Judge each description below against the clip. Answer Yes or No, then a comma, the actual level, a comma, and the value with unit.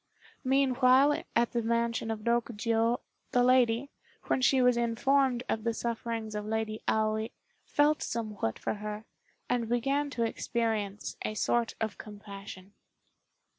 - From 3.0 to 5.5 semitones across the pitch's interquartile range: No, narrow, 2.4 semitones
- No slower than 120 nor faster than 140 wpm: Yes, slow, 135 wpm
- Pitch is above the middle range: Yes, high, 230 Hz